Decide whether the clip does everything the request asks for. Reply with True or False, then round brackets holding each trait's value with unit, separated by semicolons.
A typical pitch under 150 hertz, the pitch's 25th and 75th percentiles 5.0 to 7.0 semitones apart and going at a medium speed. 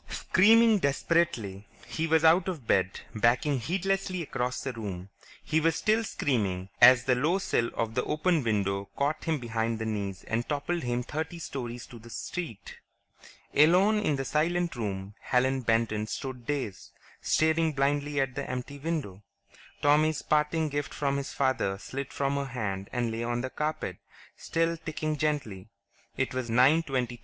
True (135 Hz; 5.3 semitones; 165 wpm)